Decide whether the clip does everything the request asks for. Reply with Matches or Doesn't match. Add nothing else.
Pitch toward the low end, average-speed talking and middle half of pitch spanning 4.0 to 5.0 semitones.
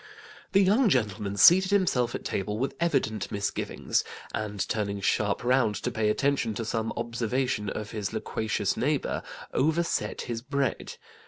Matches